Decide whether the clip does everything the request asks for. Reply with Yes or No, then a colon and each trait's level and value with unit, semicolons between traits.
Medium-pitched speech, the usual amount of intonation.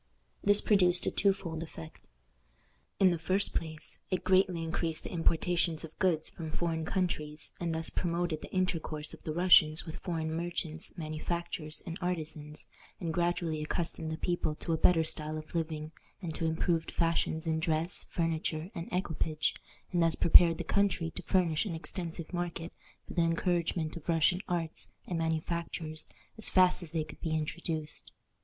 No: medium, 165 Hz; narrow, 1.8 semitones